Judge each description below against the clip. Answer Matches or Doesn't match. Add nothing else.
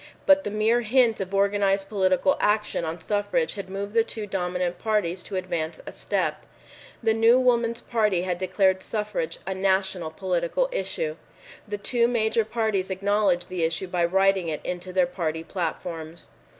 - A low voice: Doesn't match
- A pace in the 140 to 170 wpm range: Matches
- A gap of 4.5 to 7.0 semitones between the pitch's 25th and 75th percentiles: Doesn't match